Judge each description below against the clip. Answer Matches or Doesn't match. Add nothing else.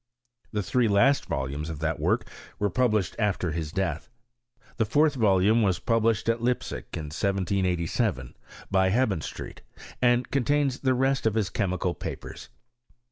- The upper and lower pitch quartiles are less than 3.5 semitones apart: Doesn't match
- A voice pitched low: Matches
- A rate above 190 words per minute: Doesn't match